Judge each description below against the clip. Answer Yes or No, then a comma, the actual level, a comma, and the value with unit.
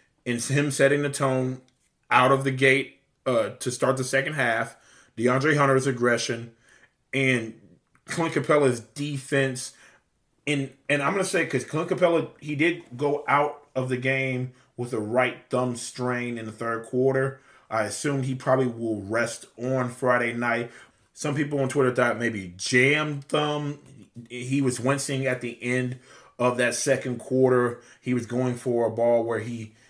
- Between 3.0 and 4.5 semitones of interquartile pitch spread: No, narrow, 2.5 semitones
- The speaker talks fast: No, average, 165 wpm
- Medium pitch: No, low, 130 Hz